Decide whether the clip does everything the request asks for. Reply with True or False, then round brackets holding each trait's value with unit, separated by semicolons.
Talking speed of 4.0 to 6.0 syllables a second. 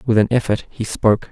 False (6.4 syllables/s)